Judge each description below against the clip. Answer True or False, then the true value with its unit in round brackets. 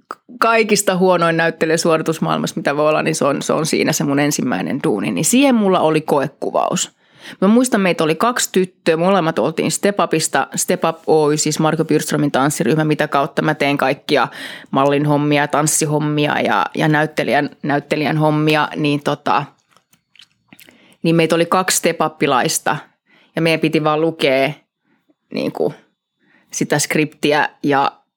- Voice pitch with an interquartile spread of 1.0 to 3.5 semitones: True (3.2 semitones)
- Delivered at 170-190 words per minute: False (145 wpm)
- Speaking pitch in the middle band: True (160 Hz)